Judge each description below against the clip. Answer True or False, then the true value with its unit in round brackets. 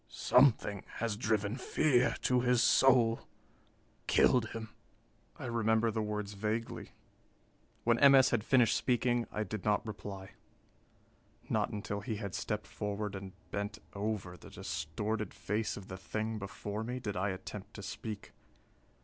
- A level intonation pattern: True (2.3 semitones)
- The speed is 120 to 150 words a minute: True (145 wpm)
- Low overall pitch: True (110 Hz)